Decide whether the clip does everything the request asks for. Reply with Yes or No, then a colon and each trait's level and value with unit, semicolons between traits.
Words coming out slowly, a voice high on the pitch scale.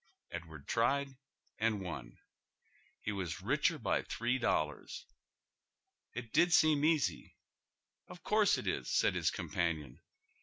No: slow, 125 wpm; low, 115 Hz